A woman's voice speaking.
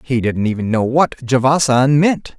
No: male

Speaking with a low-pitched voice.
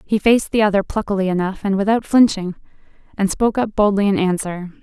No: high, 200 Hz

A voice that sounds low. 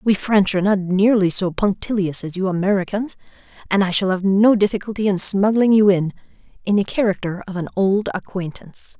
No: high, 195 Hz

